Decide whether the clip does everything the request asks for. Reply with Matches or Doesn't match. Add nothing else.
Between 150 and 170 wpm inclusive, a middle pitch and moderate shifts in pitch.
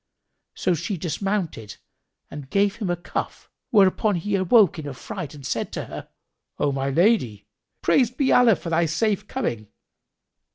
Doesn't match